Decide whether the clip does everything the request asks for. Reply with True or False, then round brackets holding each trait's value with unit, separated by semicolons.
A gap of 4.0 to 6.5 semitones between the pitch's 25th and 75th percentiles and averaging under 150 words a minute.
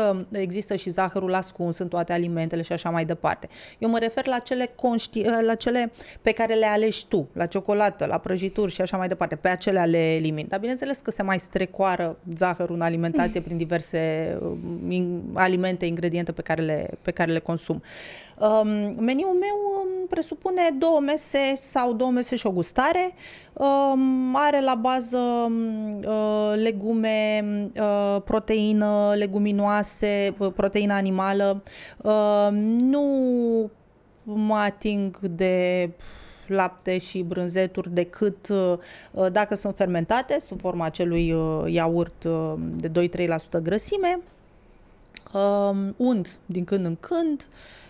True (4.3 semitones; 125 wpm)